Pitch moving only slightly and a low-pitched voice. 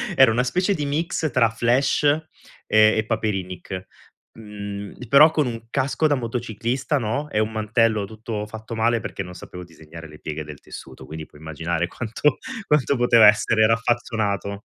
No: average, 3.7 semitones; low, 110 Hz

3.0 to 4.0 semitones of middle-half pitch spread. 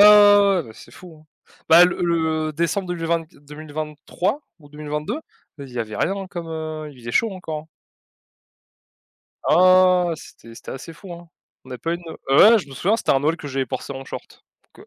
Yes: average, 3.7 semitones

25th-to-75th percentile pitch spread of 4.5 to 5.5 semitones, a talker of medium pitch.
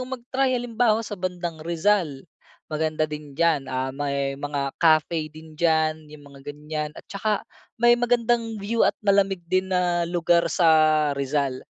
Yes: average, 4.9 semitones; medium, 165 Hz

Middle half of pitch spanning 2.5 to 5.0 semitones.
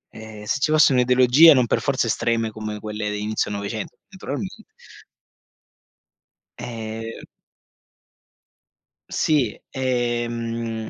Yes: average, 2.9 semitones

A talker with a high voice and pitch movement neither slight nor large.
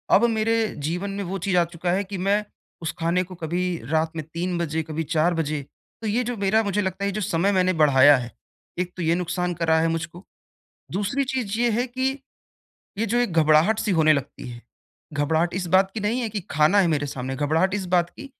No: medium, 180 Hz; average, 4.1 semitones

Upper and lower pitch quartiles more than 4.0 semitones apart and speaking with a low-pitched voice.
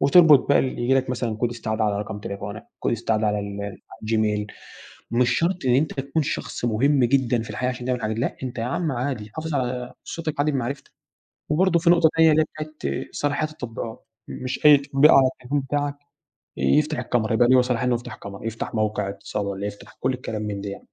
Yes: average, 4.7 semitones; low, 125 Hz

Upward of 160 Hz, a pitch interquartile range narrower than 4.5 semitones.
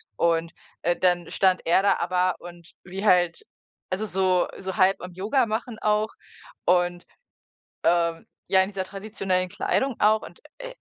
Yes: medium, 185 Hz; average, 2.8 semitones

